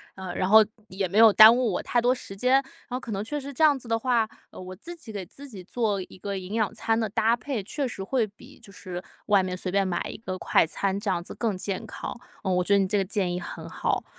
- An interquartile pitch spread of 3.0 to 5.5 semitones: Yes, average, 3.9 semitones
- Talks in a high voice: Yes, high, 205 Hz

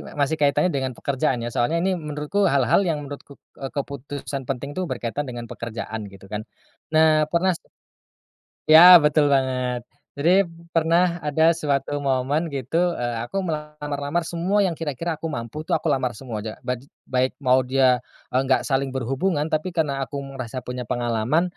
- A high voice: No, medium, 140 Hz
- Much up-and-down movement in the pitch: No, average, 3.9 semitones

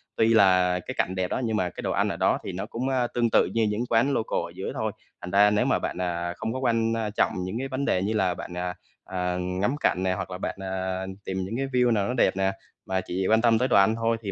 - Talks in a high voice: No, low, 100 Hz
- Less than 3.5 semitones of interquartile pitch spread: No, average, 3.8 semitones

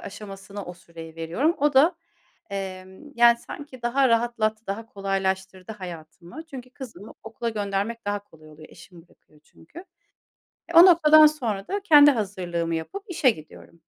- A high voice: Yes, high, 205 Hz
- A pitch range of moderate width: No, wide, 5.9 semitones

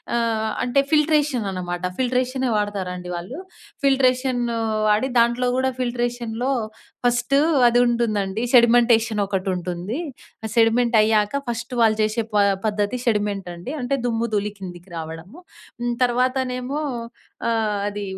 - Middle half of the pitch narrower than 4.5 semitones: Yes, average, 3.3 semitones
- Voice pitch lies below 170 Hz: No, high, 235 Hz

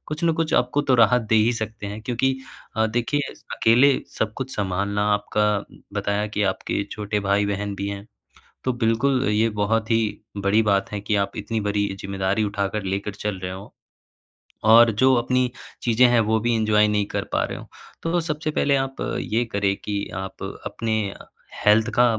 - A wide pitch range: No, average, 3.1 semitones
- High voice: No, low, 110 Hz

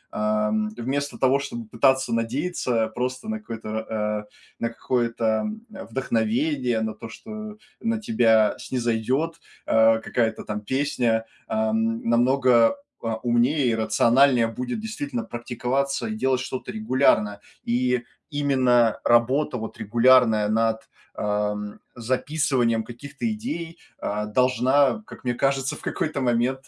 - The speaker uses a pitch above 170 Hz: No, low, 125 Hz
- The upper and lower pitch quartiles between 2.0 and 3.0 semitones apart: No, average, 3.7 semitones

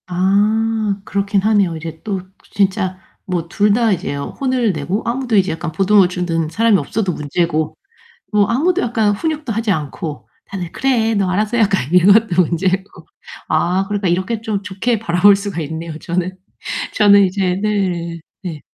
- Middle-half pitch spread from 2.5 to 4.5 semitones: Yes, average, 3.5 semitones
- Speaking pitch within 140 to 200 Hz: Yes, high, 195 Hz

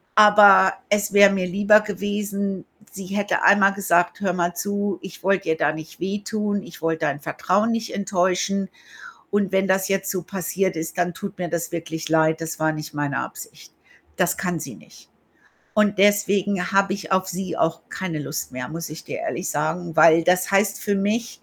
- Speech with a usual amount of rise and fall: Yes, average, 3.2 semitones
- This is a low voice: No, high, 190 Hz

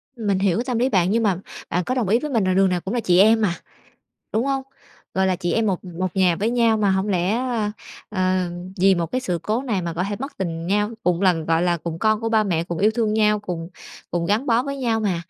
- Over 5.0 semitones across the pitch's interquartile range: No, average, 4.0 semitones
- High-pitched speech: Yes, high, 200 Hz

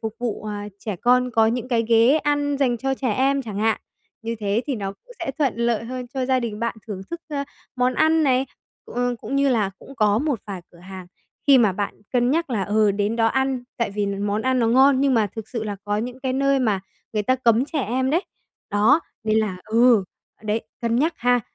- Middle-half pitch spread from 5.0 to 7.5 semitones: No, average, 3.7 semitones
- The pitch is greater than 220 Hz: Yes, high, 235 Hz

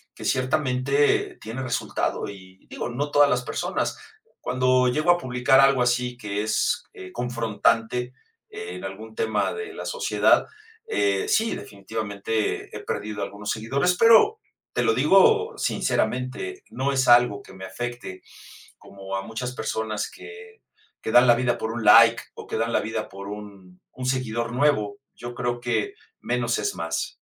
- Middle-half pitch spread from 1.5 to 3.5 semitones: No, average, 4.2 semitones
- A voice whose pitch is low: Yes, low, 120 Hz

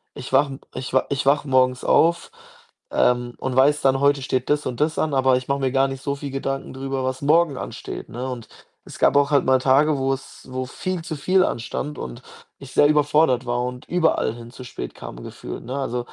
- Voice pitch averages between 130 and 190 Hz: Yes, low, 135 Hz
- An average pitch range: No, narrow, 2.1 semitones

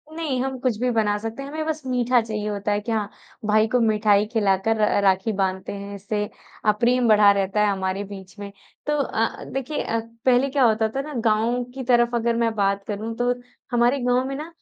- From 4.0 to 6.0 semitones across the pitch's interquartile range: No, average, 3.3 semitones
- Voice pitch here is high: Yes, high, 225 Hz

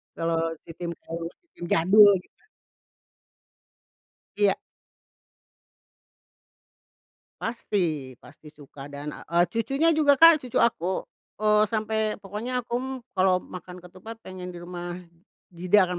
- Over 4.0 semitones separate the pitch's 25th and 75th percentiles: Yes, average, 4.4 semitones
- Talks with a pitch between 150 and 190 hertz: Yes, medium, 185 Hz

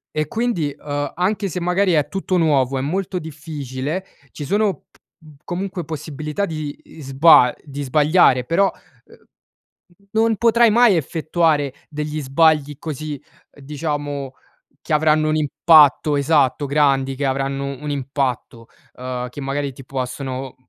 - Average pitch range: Yes, average, 3.3 semitones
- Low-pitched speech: No, medium, 150 Hz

